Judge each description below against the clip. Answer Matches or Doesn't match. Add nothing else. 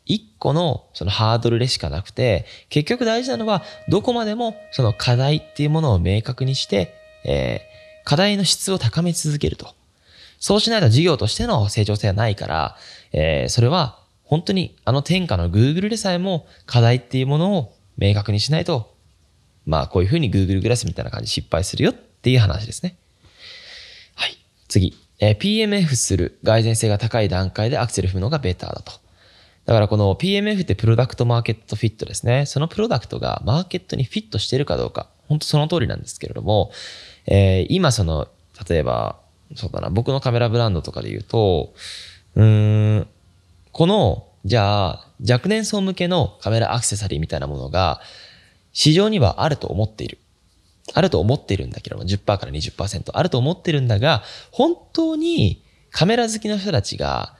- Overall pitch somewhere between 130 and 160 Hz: Doesn't match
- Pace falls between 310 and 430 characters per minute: Matches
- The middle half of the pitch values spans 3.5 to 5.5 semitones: Doesn't match